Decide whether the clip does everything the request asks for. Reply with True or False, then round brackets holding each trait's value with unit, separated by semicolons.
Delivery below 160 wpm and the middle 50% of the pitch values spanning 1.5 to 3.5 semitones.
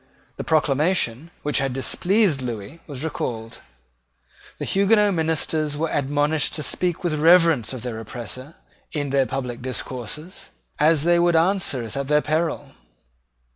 False (140 wpm; 4.3 semitones)